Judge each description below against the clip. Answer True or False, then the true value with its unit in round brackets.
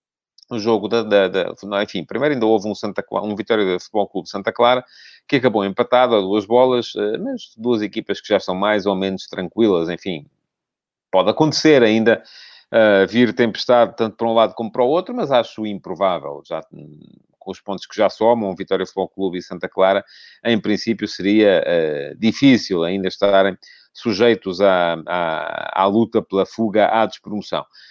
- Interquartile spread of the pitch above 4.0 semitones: False (3.2 semitones)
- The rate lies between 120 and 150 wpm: False (175 wpm)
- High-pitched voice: False (105 Hz)